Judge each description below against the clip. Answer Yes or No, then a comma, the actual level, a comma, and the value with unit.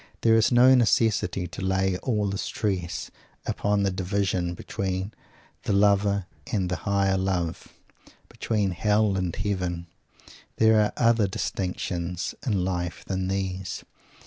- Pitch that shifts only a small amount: Yes, narrow, 2.2 semitones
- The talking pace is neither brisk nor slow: No, slow, 130 wpm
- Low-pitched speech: Yes, very low, 95 Hz